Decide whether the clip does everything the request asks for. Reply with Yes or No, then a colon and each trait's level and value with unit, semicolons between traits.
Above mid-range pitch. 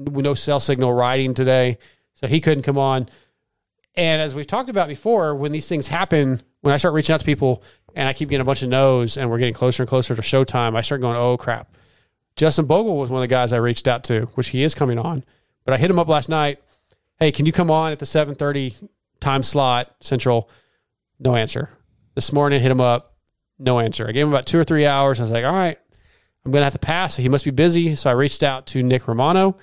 No: low, 135 Hz